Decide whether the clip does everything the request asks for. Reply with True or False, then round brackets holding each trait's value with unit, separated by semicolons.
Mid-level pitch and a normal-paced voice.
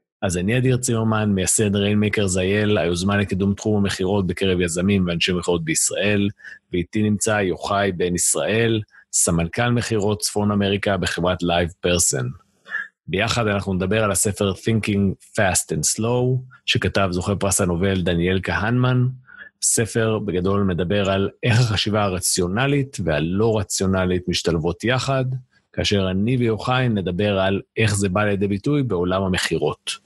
False (100 Hz; 130 wpm)